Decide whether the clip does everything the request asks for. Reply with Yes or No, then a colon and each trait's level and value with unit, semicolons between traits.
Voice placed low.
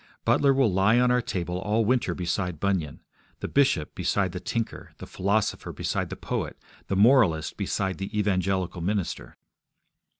Yes: very low, 95 Hz